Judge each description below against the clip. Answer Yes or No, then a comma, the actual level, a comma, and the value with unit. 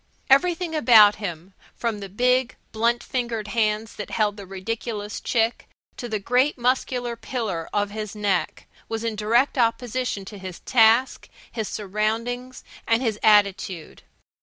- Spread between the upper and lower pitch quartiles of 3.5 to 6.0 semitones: No, average, 2.9 semitones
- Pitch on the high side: Yes, high, 225 Hz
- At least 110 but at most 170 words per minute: Yes, average, 140 wpm